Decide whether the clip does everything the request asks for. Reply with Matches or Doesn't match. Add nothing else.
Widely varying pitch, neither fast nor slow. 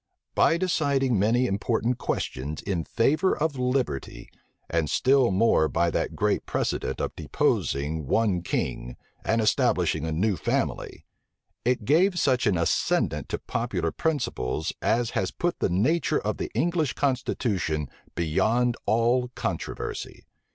Doesn't match